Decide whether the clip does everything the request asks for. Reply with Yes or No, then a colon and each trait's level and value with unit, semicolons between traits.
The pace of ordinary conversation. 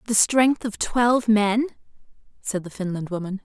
Yes: average, 155 wpm